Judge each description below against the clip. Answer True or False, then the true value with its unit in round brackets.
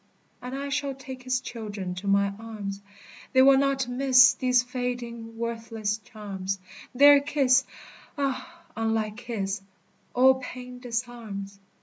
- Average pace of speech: False (125 wpm)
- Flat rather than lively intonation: False (3.3 semitones)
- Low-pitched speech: False (245 Hz)